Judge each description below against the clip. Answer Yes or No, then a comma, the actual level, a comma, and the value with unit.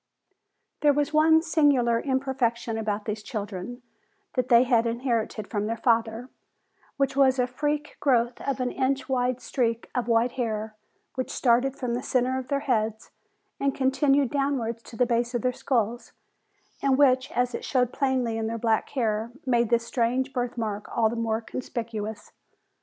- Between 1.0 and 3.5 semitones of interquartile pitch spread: Yes, narrow, 2.6 semitones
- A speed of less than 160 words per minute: No, average, 170 wpm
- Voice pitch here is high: Yes, high, 245 Hz